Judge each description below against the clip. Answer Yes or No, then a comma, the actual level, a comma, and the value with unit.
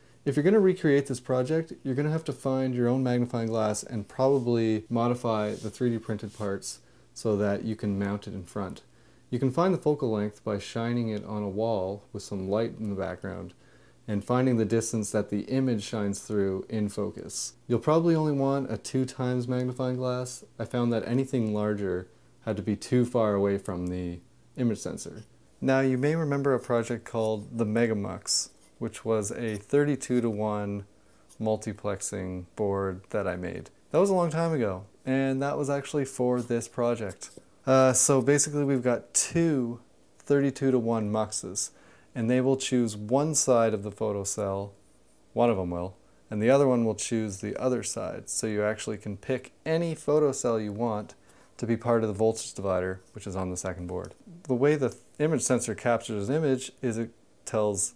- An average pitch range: Yes, average, 3.9 semitones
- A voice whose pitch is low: Yes, low, 115 Hz